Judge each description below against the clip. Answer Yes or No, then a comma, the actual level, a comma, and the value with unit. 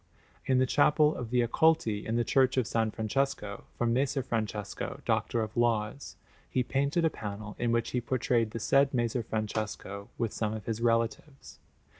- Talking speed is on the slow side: No, average, 175 wpm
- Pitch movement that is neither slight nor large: Yes, average, 3.2 semitones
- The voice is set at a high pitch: No, low, 115 Hz